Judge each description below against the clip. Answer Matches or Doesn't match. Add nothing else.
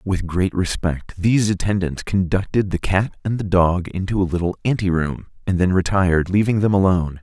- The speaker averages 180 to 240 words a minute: Matches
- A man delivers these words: Matches